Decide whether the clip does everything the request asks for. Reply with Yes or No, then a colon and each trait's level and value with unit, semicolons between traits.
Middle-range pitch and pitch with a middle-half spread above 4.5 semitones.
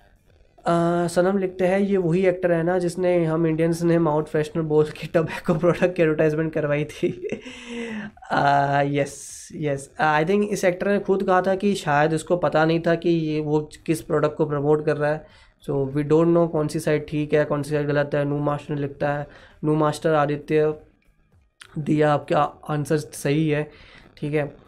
No: medium, 155 Hz; average, 2.7 semitones